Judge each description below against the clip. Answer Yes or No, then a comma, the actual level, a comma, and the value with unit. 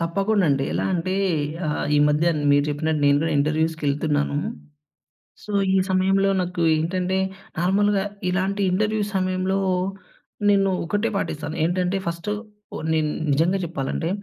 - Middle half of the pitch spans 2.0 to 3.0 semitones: No, average, 3.8 semitones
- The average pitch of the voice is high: No, medium, 175 Hz